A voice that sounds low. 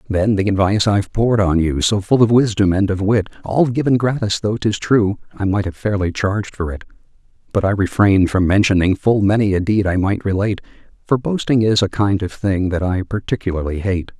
Yes: low, 100 Hz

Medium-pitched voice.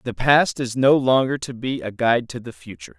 No: low, 125 Hz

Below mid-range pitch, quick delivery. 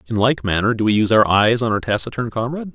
Yes: low, 115 Hz; fast, 260 wpm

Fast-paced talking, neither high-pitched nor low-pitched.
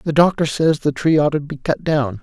Yes: fast, 270 wpm; medium, 150 Hz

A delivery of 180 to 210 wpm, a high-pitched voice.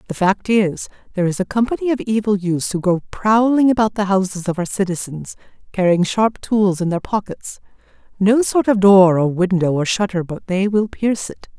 Yes: average, 190 wpm; high, 195 Hz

